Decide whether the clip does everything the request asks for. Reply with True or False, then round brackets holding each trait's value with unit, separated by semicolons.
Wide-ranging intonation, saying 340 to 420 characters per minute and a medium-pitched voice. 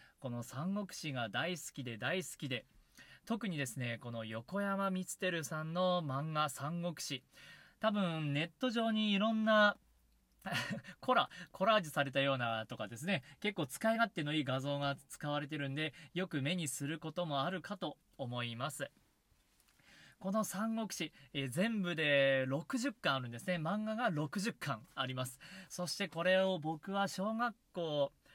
False (6.1 semitones; 280 characters per minute; 160 Hz)